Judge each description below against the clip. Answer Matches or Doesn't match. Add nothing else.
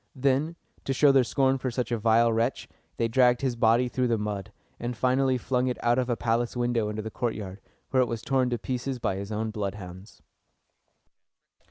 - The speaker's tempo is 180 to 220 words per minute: Matches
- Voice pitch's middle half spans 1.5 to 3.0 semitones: Matches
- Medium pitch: Doesn't match